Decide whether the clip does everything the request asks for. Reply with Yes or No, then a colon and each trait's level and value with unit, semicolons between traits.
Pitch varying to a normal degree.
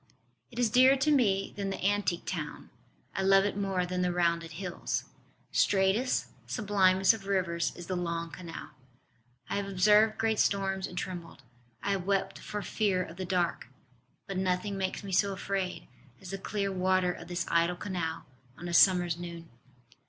No: narrow, 2.1 semitones